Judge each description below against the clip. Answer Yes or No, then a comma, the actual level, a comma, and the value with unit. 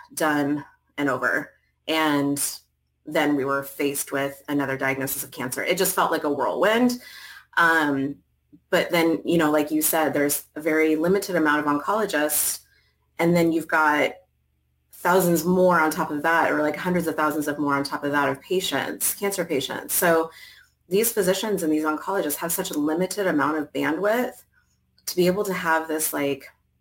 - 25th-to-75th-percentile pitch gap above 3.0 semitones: Yes, average, 3.7 semitones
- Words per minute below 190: Yes, average, 175 wpm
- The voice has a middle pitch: Yes, medium, 155 Hz